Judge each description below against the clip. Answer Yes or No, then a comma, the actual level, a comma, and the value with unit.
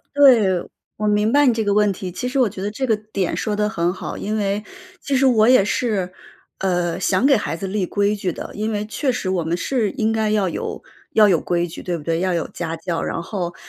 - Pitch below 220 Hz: Yes, high, 205 Hz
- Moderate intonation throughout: Yes, average, 3.5 semitones